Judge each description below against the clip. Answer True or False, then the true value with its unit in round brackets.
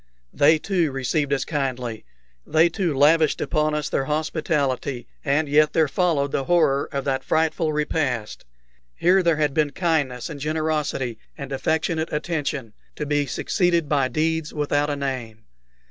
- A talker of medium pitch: True (150 Hz)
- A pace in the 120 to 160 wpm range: True (150 wpm)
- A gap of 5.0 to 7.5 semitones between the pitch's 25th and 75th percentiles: False (2.6 semitones)